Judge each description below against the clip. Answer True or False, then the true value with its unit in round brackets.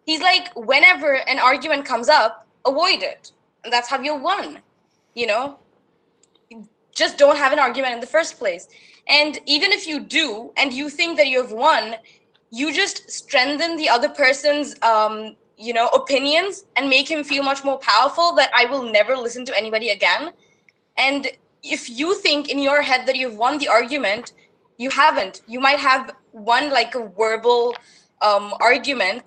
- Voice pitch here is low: False (270 Hz)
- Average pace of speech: True (170 wpm)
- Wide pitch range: False (4.0 semitones)